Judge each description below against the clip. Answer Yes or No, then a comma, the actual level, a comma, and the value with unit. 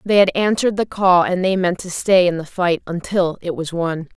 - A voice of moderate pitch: Yes, medium, 180 Hz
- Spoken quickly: Yes, fast, 245 wpm